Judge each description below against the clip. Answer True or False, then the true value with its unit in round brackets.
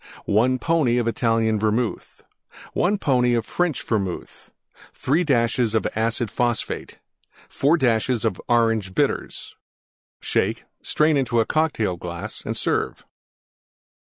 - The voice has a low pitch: True (120 Hz)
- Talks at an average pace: False (100 wpm)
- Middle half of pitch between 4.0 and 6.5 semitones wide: False (3.4 semitones)